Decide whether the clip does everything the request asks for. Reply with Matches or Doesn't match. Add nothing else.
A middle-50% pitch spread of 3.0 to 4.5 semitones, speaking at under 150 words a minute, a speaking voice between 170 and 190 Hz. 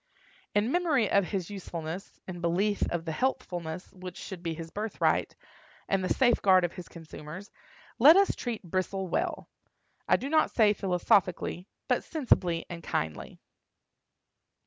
Matches